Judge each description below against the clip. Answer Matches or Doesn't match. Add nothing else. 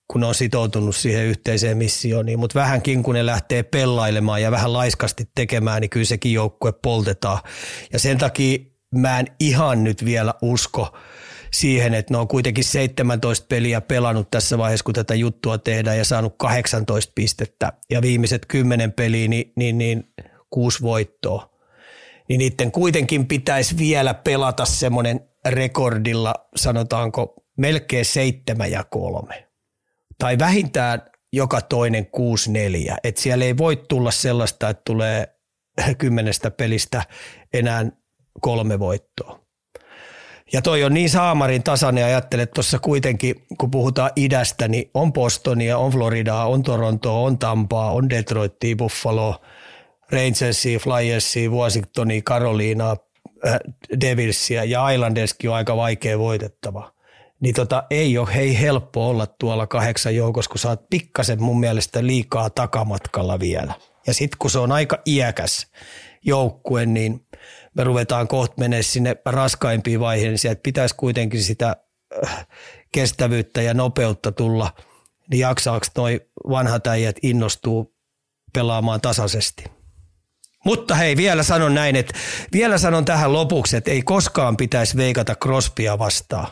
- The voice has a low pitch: Matches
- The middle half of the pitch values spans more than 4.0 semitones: Doesn't match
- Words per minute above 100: Matches